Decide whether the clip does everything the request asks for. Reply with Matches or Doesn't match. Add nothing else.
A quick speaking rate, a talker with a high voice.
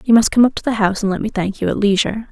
Matches